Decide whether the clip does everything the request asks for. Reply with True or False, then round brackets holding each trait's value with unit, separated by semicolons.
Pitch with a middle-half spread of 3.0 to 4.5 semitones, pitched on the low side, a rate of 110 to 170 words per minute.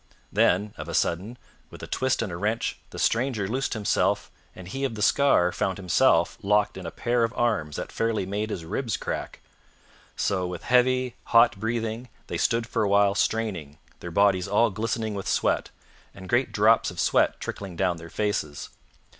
False (3.7 semitones; 105 Hz; 185 wpm)